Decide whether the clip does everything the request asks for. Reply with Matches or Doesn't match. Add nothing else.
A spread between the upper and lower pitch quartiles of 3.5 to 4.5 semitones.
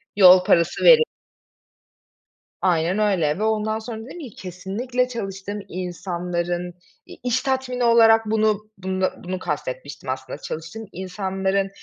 Matches